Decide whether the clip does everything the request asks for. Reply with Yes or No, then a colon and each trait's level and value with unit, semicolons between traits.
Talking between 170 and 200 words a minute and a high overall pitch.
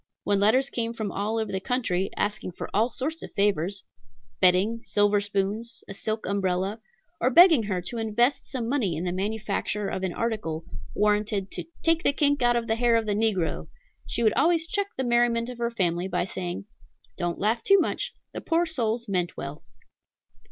Yes: average, 190 wpm; high, 215 Hz